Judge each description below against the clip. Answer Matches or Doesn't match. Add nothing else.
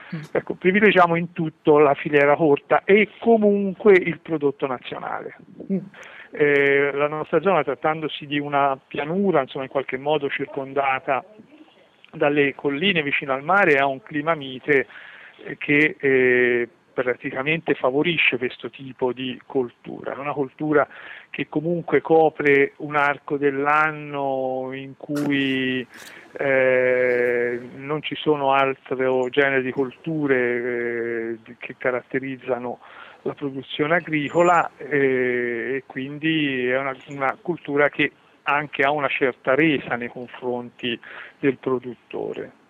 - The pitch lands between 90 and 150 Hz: Matches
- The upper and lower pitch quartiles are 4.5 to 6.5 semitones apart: Doesn't match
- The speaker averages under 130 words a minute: Matches